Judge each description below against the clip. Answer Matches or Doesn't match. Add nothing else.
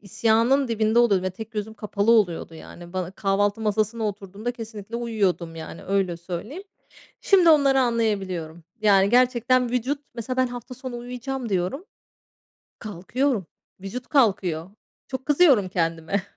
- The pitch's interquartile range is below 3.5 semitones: Doesn't match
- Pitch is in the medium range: Doesn't match